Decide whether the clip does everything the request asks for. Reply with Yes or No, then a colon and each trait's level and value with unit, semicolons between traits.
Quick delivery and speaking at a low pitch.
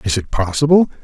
No: average, 175 wpm; low, 120 Hz